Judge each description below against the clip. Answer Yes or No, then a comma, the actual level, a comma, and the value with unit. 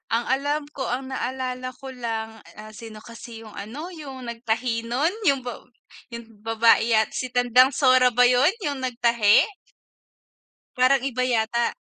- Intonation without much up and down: Yes, narrow, 2.3 semitones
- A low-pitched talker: No, high, 245 Hz